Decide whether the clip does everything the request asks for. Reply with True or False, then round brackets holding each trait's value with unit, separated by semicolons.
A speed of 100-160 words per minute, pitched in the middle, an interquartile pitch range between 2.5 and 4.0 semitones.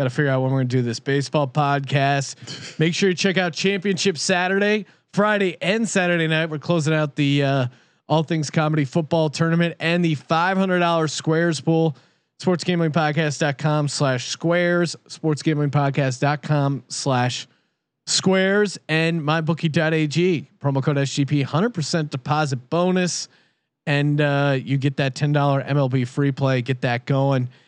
True (150 wpm; 155 Hz; 3.4 semitones)